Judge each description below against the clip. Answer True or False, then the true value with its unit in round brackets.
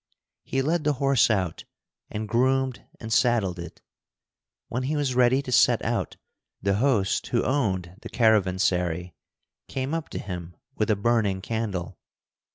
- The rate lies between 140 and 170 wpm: True (150 wpm)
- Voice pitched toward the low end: True (110 Hz)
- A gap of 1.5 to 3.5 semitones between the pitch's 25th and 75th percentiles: False (5.6 semitones)